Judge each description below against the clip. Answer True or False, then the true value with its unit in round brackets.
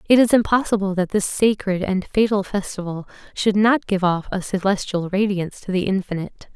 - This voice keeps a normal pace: True (175 wpm)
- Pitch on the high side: True (195 Hz)